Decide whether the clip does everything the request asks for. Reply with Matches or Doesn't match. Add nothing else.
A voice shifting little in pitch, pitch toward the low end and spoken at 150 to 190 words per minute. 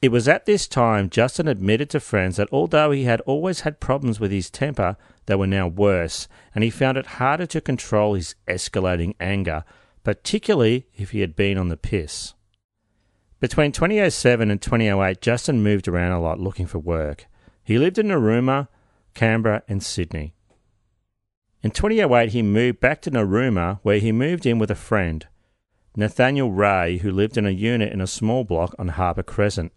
Doesn't match